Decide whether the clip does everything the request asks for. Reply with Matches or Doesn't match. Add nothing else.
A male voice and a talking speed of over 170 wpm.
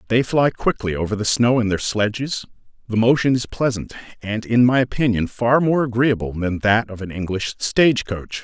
Matches